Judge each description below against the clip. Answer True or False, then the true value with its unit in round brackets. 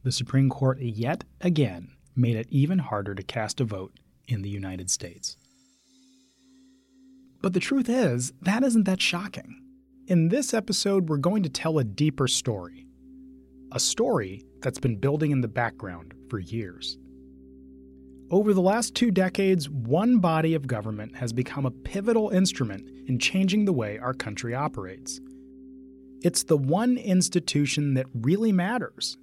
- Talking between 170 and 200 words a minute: False (150 wpm)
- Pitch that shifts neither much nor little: False (8.7 semitones)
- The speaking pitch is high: False (135 Hz)